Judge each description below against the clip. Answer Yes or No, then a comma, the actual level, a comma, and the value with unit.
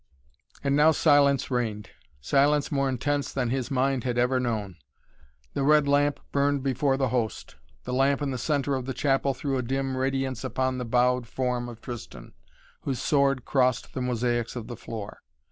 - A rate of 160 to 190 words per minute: Yes, average, 180 wpm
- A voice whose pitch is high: No, low, 130 Hz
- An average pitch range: No, narrow, 2.2 semitones